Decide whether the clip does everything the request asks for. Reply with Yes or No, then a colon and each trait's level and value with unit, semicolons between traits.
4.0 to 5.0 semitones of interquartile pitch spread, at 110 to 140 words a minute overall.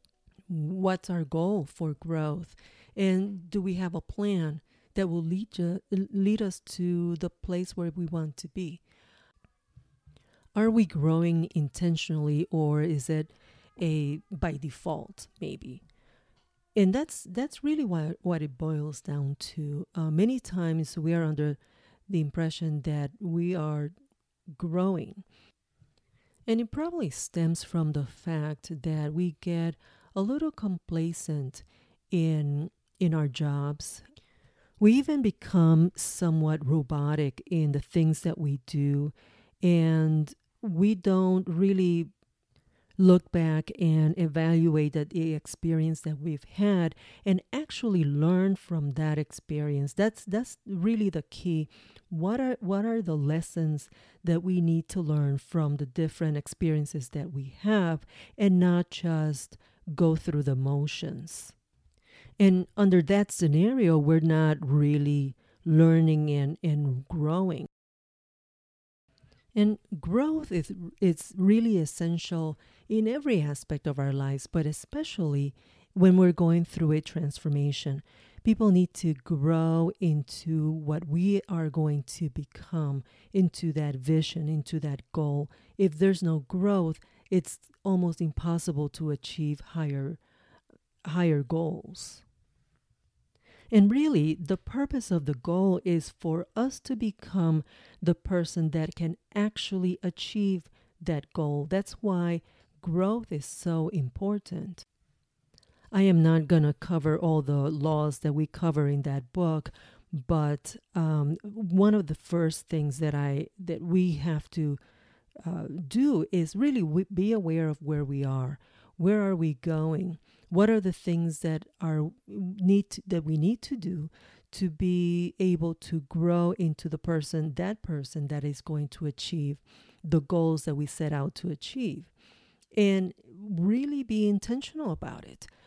No: average, 3.4 semitones; slow, 135 wpm